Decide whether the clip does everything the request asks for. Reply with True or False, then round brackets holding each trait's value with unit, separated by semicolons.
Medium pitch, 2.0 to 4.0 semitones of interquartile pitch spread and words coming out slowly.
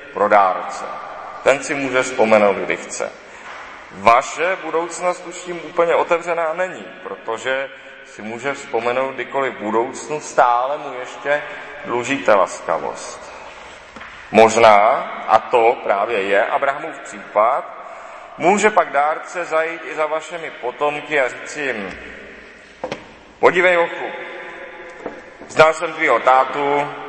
False (145 Hz; 4.8 semitones; 110 wpm)